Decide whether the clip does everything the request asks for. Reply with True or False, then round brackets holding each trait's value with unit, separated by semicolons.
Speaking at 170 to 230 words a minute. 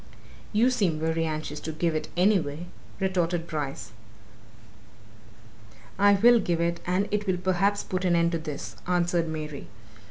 False (150 wpm)